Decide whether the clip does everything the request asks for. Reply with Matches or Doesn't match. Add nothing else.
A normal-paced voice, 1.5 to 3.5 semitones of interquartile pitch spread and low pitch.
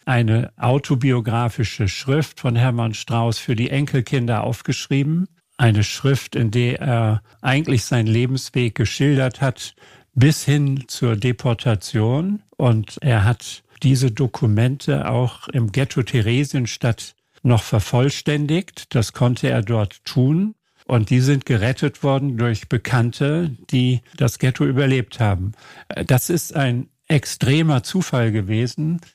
Doesn't match